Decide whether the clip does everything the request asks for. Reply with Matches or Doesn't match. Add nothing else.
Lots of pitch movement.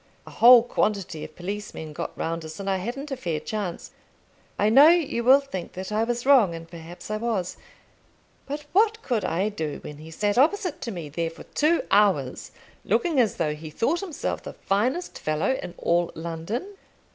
Matches